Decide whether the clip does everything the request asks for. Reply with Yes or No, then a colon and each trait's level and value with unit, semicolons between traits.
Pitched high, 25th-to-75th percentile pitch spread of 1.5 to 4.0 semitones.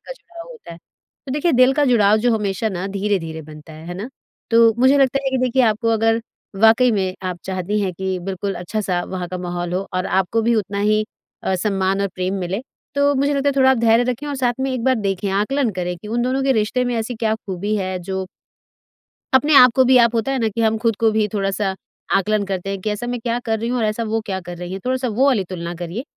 No: high, 215 Hz; average, 4.5 semitones